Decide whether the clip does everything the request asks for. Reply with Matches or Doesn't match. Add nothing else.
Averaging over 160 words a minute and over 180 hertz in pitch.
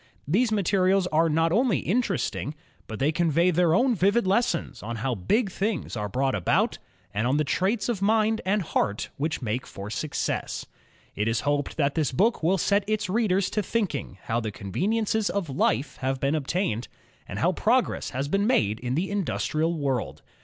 Doesn't match